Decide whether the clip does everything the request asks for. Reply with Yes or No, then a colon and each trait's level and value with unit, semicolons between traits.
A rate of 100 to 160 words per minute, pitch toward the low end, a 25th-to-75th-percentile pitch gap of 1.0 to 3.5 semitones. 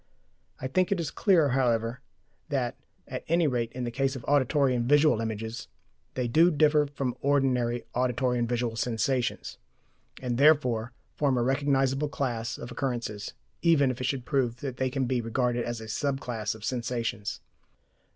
No: average, 170 wpm; low, 125 Hz; average, 2.9 semitones